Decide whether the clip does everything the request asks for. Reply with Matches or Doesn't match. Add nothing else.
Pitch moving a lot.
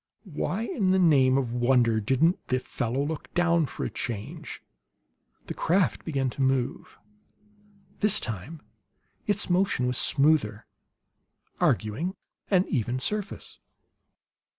Matches